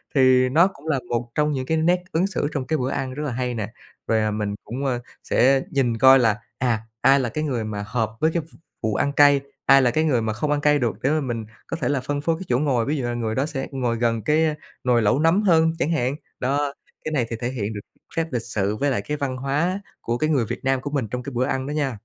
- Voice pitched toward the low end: Yes, low, 130 Hz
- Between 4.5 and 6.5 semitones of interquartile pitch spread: No, average, 3.7 semitones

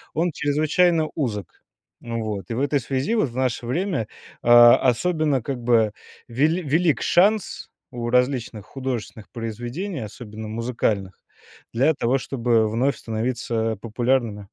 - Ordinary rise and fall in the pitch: Yes, average, 4.2 semitones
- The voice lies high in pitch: No, low, 120 Hz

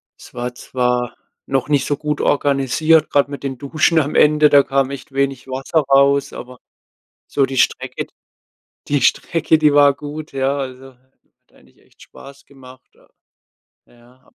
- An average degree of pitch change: No, narrow, 1.9 semitones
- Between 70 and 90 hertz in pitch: No, medium, 140 Hz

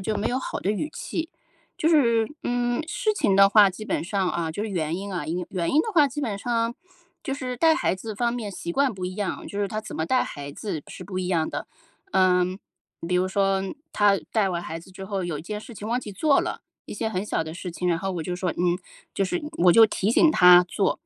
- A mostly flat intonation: No, average, 4.5 semitones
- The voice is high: Yes, high, 200 Hz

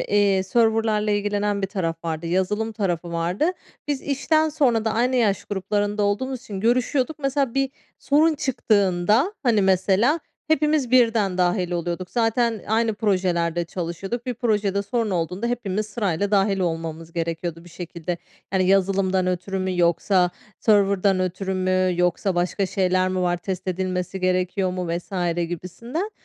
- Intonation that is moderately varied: Yes, average, 3.8 semitones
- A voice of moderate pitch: No, high, 195 Hz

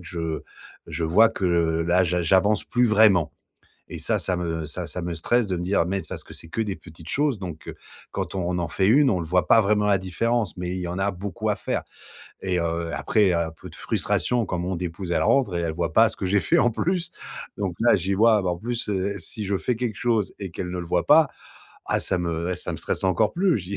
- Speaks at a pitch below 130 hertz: Yes, very low, 95 Hz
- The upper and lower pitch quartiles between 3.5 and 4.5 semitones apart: Yes, average, 3.9 semitones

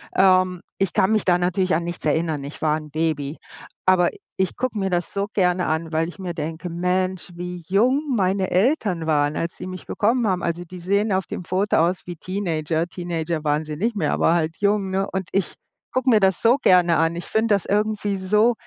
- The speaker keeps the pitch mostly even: No, average, 3.1 semitones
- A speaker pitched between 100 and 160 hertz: No, medium, 180 Hz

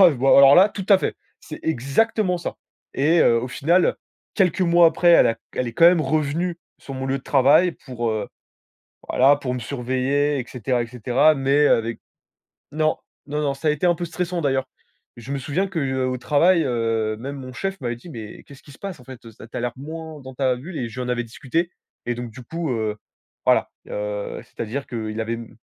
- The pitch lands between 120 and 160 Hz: Yes, low, 135 Hz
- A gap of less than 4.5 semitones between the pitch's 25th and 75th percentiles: No, average, 4.8 semitones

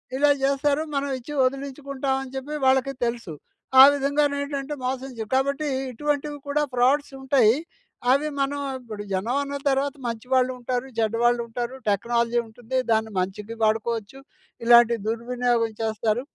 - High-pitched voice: Yes, very high, 255 Hz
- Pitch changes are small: No, average, 3.2 semitones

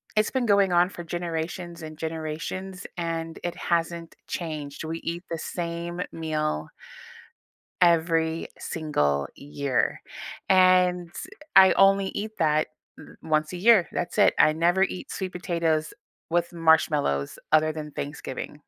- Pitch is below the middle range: No, medium, 165 Hz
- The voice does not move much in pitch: Yes, narrow, 2.3 semitones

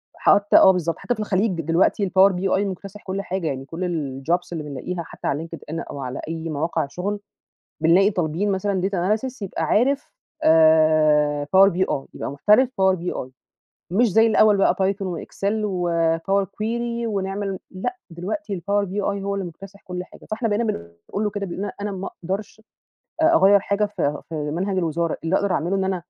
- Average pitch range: Yes, average, 3.6 semitones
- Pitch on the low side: No, high, 190 Hz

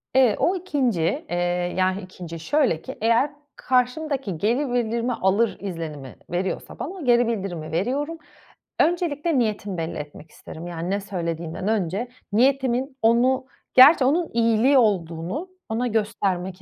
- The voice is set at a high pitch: Yes, high, 225 Hz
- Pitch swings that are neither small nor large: No, wide, 6.8 semitones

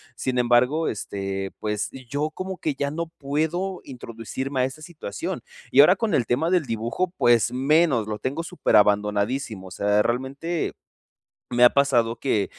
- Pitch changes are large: Yes, wide, 5.7 semitones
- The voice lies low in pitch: Yes, low, 130 Hz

